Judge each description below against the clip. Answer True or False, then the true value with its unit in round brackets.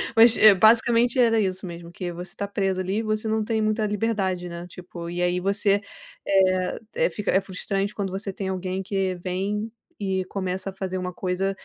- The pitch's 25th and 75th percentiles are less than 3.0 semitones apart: True (2.5 semitones)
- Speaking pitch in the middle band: False (195 Hz)